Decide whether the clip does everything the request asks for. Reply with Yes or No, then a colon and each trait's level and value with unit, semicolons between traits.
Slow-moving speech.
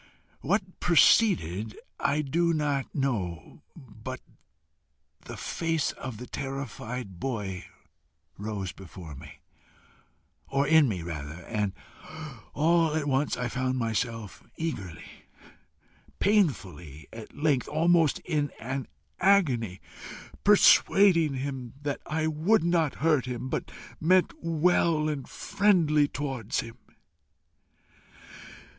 Yes: slow, 105 wpm